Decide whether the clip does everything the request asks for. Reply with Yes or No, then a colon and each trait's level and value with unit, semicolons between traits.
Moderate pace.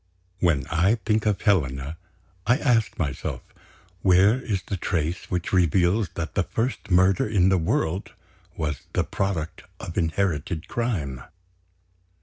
No: slow, 130 wpm